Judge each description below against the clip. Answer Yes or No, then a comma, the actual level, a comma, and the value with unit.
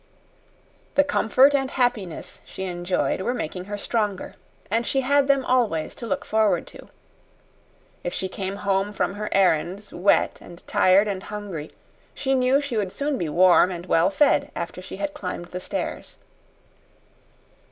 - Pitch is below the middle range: No, high, 200 Hz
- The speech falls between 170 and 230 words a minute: No, average, 160 wpm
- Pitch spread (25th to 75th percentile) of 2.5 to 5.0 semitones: No, wide, 5.6 semitones